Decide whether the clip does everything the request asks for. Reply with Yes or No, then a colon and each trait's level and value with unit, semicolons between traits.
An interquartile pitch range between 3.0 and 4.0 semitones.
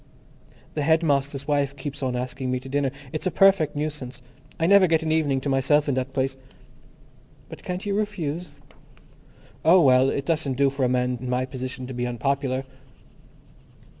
Yes: average, 3.4 semitones